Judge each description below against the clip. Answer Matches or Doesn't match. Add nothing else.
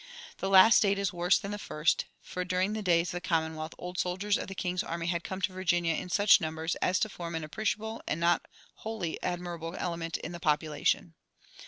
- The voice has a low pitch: Doesn't match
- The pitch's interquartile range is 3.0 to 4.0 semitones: Doesn't match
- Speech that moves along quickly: Matches